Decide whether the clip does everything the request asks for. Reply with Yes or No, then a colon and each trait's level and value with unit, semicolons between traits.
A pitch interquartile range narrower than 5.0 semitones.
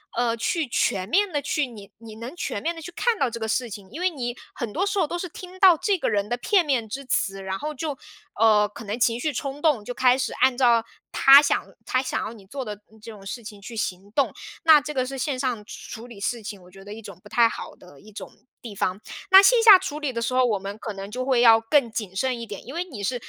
No: wide, 5.4 semitones